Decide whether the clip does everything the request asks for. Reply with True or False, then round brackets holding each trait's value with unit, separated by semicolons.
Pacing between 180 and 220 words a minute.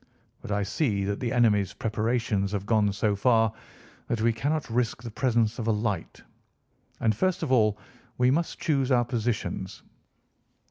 False (165 wpm)